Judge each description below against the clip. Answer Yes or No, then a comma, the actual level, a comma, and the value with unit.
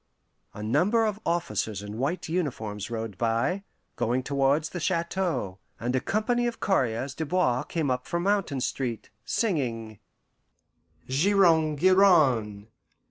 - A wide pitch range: Yes, wide, 7.9 semitones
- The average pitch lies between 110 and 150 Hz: Yes, medium, 140 Hz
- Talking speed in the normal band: No, slow, 130 wpm